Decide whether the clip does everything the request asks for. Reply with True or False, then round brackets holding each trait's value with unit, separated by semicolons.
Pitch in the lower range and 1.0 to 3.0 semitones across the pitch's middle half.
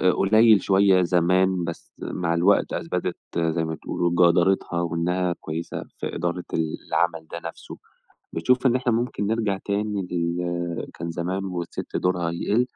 True (90 Hz; 2.5 semitones)